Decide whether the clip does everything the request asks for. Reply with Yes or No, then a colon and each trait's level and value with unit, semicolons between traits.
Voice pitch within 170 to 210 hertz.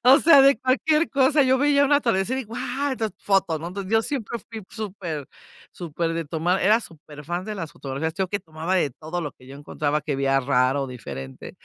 Yes: medium, 185 Hz